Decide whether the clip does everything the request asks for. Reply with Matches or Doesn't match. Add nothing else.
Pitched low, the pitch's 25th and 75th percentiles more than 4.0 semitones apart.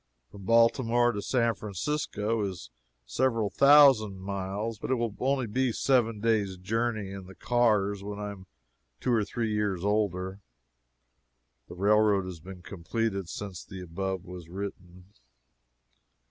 Doesn't match